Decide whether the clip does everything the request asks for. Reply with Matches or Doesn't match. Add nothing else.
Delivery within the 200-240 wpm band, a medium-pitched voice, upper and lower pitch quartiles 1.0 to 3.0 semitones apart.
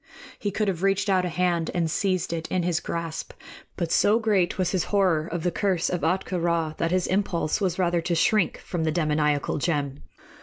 Matches